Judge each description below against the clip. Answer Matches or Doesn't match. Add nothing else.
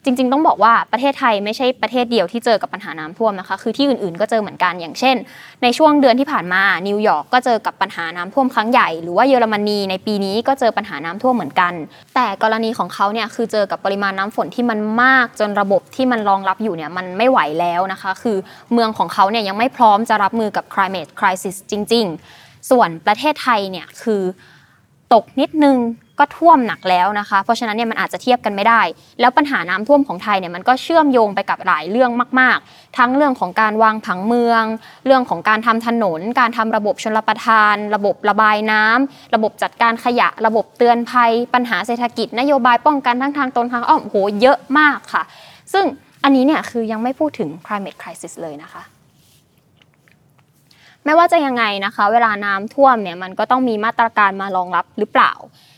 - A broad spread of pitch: Doesn't match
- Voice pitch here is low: Doesn't match